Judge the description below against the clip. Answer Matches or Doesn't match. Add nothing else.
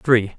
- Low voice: Matches